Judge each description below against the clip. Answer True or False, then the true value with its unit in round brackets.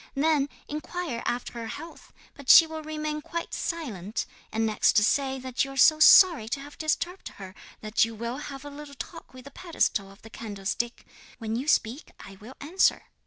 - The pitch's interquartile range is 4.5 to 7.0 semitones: True (5.4 semitones)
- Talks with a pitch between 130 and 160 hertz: False (270 Hz)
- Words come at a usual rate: True (190 wpm)